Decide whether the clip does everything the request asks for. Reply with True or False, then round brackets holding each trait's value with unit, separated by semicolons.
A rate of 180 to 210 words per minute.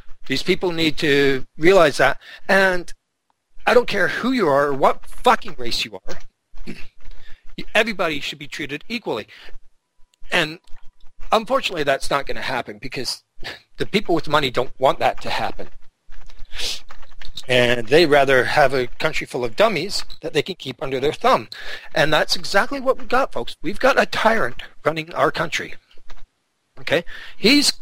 False (160 wpm)